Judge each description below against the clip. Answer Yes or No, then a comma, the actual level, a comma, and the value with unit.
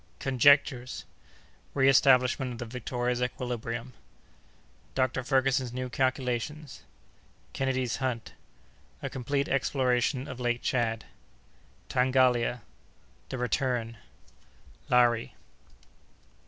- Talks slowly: Yes, slow, 55 wpm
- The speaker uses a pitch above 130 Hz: No, low, 125 Hz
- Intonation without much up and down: Yes, narrow, 1.6 semitones